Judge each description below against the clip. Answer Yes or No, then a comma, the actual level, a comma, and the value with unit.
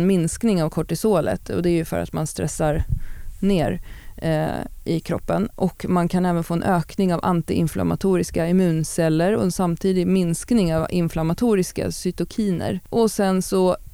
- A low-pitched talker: No, medium, 175 Hz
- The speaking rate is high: No, average, 150 wpm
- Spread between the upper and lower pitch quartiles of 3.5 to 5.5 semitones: No, average, 2.9 semitones